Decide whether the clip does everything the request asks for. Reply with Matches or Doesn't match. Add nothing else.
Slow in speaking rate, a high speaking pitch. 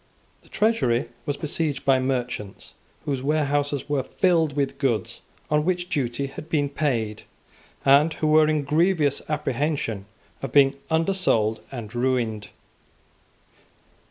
Doesn't match